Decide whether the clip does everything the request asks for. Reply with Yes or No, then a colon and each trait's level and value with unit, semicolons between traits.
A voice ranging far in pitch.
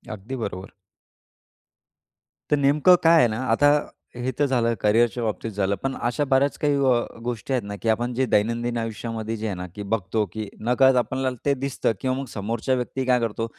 No: average, 3.2 semitones